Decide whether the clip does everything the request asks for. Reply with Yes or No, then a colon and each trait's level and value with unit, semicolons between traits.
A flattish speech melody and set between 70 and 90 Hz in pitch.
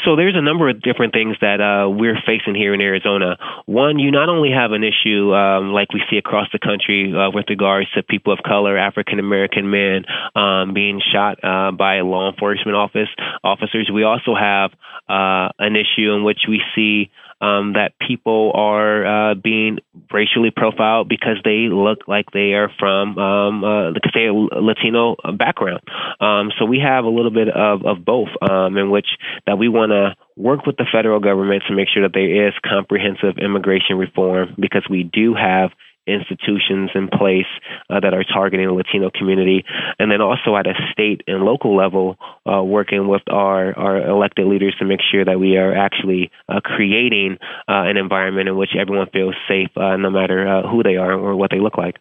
No: narrow, 1.7 semitones; low, 100 Hz